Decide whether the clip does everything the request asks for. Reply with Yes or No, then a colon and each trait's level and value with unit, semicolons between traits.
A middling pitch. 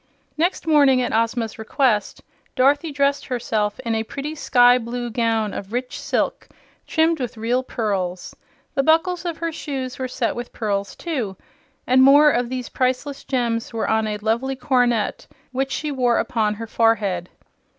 No: high, 245 Hz